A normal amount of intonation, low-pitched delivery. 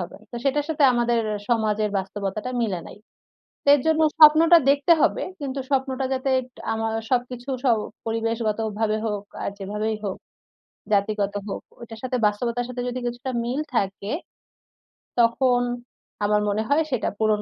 No: average, 3.6 semitones; high, 230 Hz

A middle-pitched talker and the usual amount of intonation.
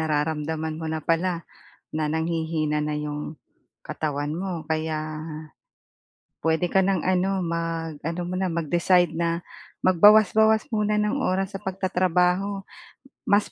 Yes: medium, 170 Hz; average, 3.0 semitones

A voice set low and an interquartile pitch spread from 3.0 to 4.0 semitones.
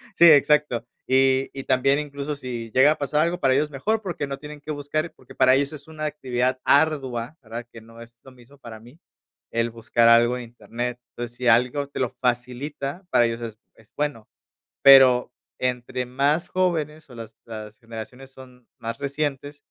Yes: low, 130 Hz; average, 3.4 semitones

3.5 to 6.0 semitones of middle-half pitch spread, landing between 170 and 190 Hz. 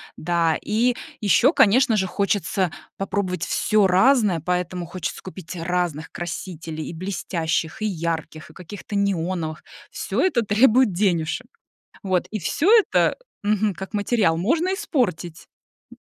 Yes: average, 4.1 semitones; medium, 185 Hz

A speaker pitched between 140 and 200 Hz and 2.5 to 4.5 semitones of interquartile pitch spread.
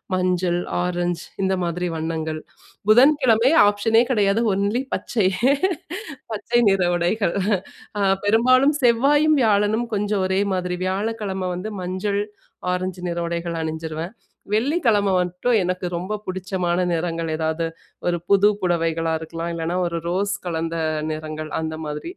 Yes: medium, 185 Hz; average, 3.9 semitones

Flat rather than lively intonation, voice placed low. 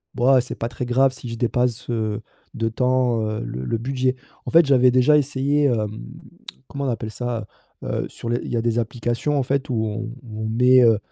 Yes: narrow, 2.3 semitones; low, 120 Hz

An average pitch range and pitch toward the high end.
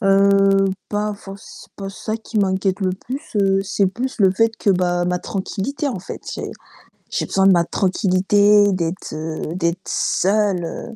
No: narrow, 1.9 semitones; high, 195 Hz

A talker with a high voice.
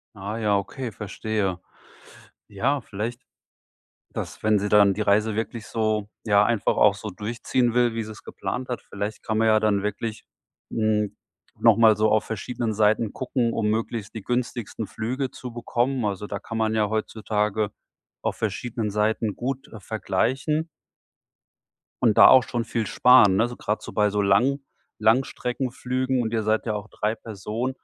No: low, 110 Hz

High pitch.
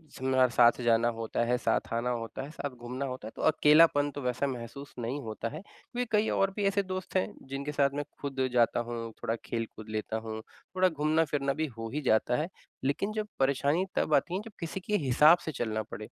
No: medium, 140 Hz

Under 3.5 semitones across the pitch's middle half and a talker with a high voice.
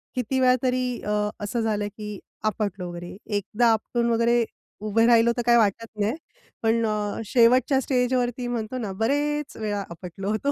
Yes: average, 2.9 semitones; high, 225 Hz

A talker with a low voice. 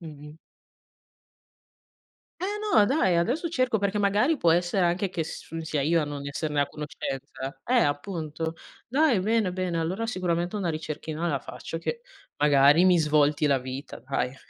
No: medium, 170 Hz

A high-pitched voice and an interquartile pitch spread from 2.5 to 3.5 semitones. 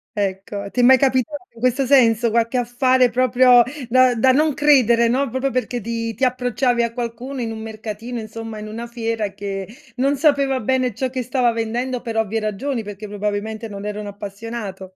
Yes: high, 235 Hz; average, 2.9 semitones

